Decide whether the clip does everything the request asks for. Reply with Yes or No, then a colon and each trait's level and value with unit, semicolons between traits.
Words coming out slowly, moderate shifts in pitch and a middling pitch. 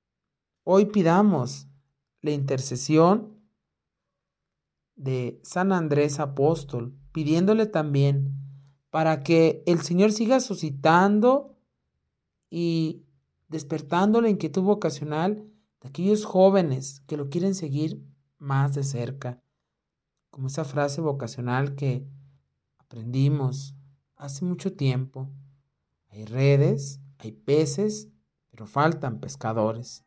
Yes: slow, 95 wpm; average, 4.0 semitones; medium, 145 Hz